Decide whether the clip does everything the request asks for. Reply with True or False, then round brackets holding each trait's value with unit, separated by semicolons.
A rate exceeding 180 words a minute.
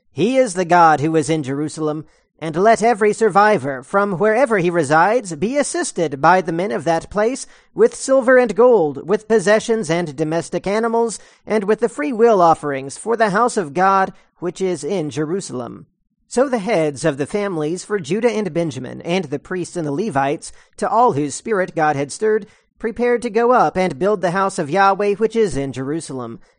True (190 wpm)